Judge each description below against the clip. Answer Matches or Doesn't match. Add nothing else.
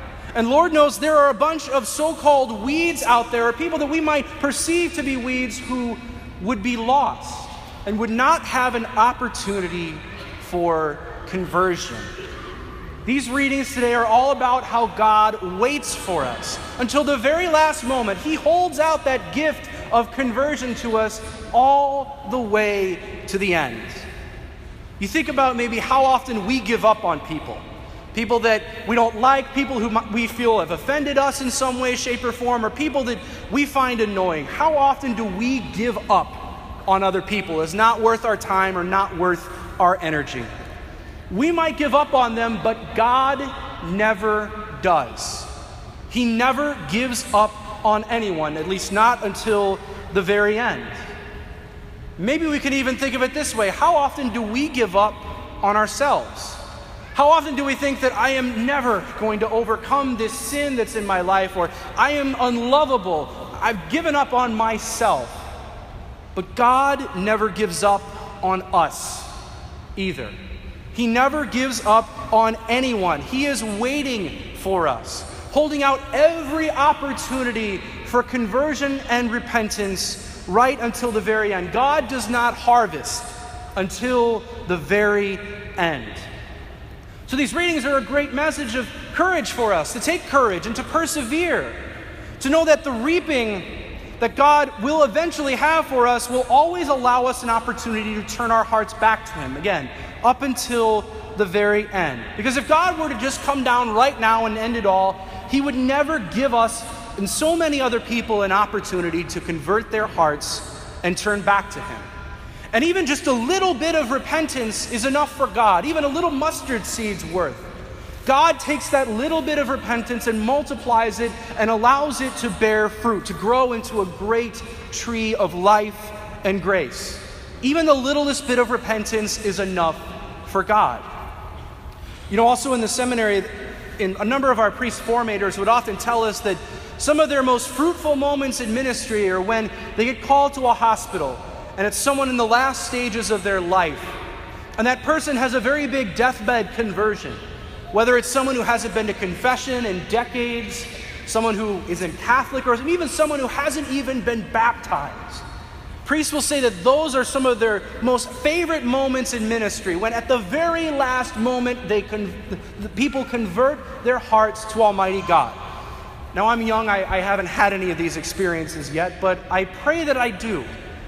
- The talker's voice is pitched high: Matches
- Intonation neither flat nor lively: Matches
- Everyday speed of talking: Matches